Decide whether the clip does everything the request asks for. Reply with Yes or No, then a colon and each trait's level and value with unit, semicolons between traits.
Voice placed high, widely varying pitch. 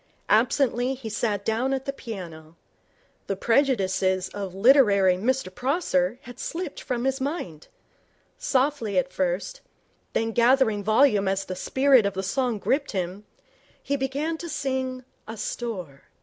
Yes: high, 235 Hz; wide, 5.7 semitones